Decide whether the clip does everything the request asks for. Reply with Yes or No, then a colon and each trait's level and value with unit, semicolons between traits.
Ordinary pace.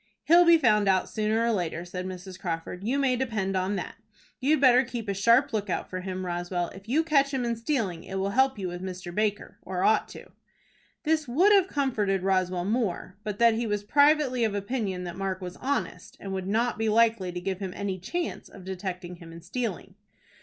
No: fast, 210 wpm